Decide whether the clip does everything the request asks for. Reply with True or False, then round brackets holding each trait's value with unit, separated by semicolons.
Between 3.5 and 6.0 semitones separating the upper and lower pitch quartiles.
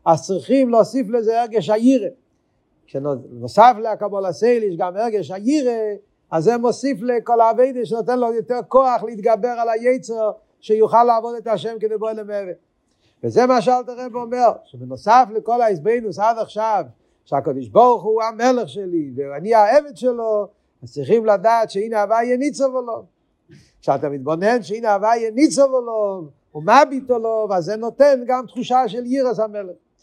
False (3.0 semitones)